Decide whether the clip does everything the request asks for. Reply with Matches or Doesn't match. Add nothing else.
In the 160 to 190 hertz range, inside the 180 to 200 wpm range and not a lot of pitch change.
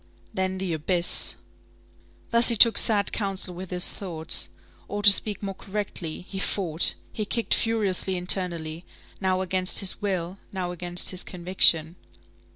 Doesn't match